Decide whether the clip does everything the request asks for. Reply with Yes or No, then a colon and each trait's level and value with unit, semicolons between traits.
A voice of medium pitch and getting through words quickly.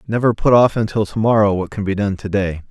No: low, 105 Hz; fast, 220 wpm